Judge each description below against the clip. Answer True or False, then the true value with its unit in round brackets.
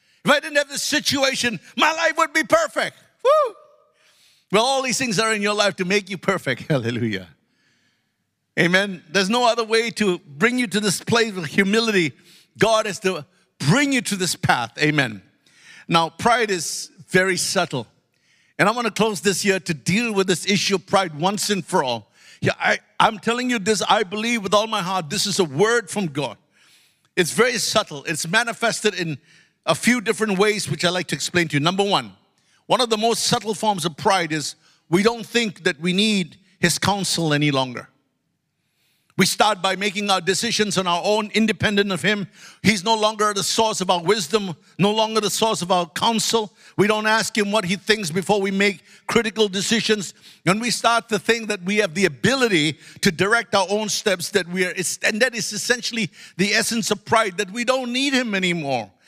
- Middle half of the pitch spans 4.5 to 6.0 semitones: False (3.7 semitones)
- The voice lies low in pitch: False (200 Hz)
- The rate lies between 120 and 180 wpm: False (200 wpm)